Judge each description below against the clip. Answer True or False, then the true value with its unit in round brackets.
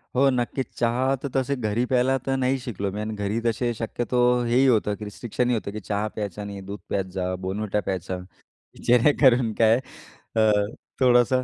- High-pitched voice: False (115 Hz)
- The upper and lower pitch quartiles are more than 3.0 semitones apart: True (3.5 semitones)